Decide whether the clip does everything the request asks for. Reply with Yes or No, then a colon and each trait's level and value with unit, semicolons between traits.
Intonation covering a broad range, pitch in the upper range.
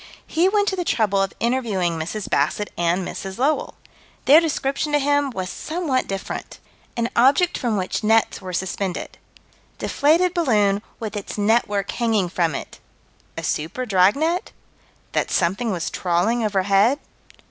Yes: wide, 6.5 semitones; high, 215 Hz